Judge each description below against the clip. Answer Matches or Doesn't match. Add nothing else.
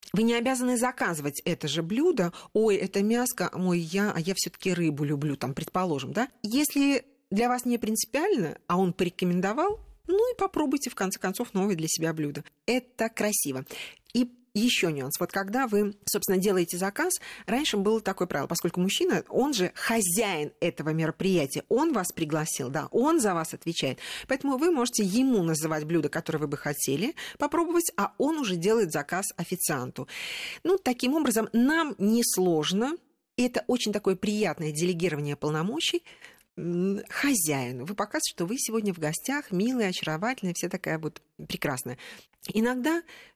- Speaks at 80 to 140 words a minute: Doesn't match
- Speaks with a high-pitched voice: Matches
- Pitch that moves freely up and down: Matches